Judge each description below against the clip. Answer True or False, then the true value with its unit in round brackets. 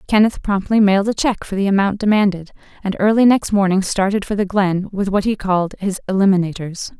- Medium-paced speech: True (195 wpm)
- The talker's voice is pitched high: True (195 Hz)